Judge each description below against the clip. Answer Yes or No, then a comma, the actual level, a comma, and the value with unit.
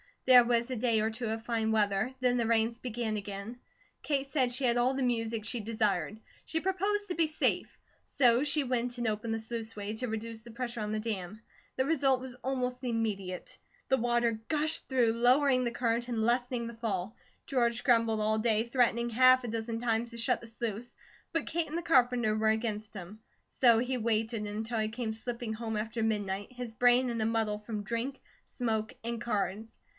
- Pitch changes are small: Yes, narrow, 2.3 semitones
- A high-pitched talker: Yes, high, 235 Hz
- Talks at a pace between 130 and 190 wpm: No, average, 200 wpm